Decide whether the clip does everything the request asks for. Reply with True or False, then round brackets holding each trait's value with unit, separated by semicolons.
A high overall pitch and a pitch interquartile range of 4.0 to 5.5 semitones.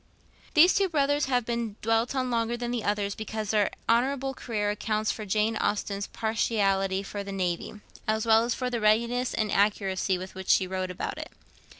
False (220 Hz; 3.0 semitones)